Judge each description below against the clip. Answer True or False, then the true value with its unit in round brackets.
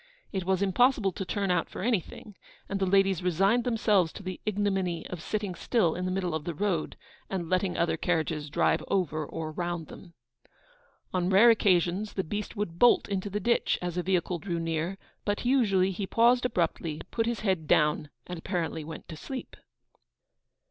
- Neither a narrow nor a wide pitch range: True (3.4 semitones)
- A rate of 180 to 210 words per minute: True (185 wpm)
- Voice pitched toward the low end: False (185 Hz)